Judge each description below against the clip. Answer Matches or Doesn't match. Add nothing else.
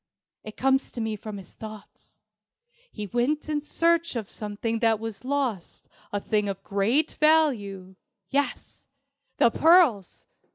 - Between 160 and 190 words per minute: Doesn't match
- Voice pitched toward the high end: Matches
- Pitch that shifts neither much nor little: Doesn't match